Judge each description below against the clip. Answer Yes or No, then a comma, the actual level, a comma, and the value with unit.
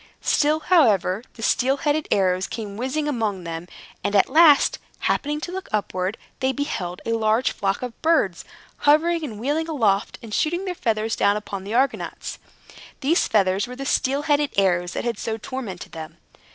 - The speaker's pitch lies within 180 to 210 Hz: No, high, 230 Hz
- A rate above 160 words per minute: Yes, average, 175 wpm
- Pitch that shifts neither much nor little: No, wide, 6.7 semitones